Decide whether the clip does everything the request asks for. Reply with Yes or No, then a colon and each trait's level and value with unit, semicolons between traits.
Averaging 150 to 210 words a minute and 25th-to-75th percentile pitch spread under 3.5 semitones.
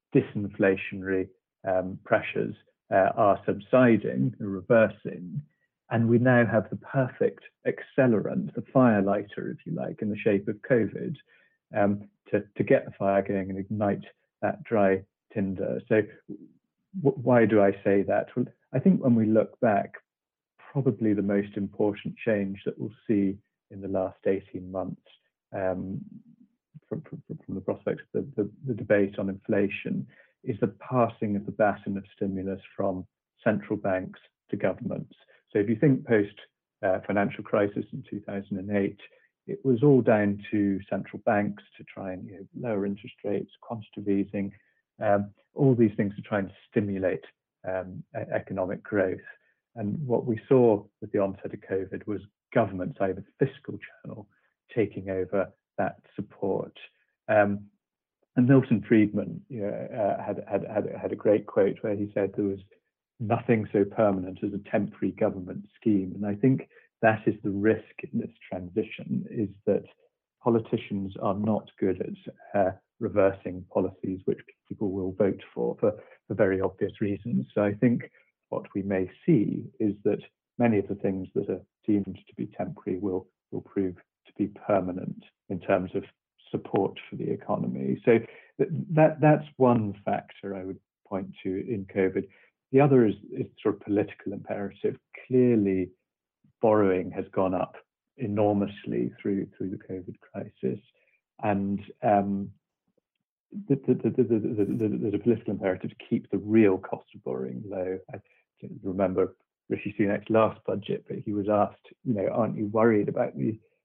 Yes: average, 160 wpm; average, 3.0 semitones